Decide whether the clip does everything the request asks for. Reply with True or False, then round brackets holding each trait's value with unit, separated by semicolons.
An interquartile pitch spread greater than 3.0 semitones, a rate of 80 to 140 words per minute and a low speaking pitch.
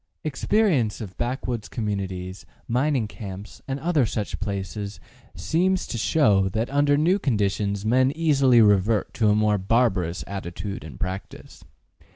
True (5.2 semitones; 135 wpm; 110 Hz)